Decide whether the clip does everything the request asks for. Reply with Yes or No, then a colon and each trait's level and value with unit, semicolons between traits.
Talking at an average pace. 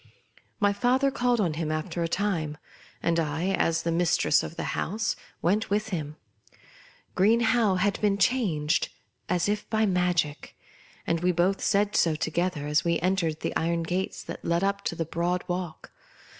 Yes: average, 175 wpm